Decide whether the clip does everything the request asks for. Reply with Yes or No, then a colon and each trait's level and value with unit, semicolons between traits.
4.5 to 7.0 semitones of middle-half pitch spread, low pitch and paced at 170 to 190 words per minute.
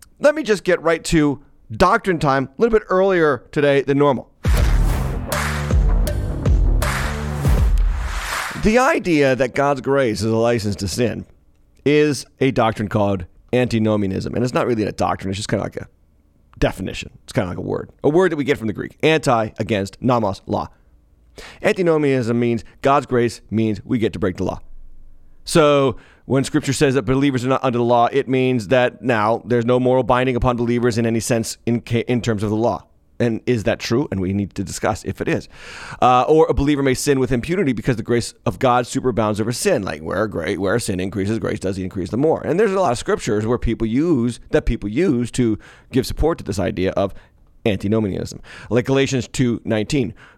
No: wide, 5.6 semitones; low, 120 Hz; average, 200 wpm